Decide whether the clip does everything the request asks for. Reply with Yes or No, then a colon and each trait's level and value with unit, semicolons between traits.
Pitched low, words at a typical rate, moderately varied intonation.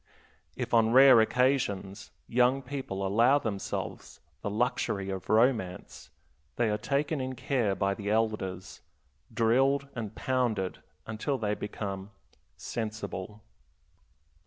No: low, 110 Hz; slow, 110 wpm; average, 4.2 semitones